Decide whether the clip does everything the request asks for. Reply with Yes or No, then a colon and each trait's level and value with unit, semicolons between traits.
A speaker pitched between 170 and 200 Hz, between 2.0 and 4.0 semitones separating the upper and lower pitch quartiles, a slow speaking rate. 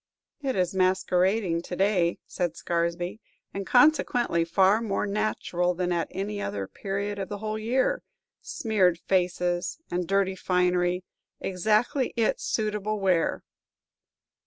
Yes: high, 190 Hz; average, 3.1 semitones; slow, 125 wpm